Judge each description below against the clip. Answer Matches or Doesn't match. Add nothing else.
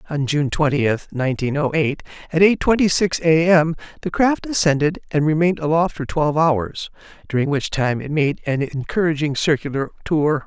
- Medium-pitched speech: Matches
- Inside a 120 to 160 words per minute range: Doesn't match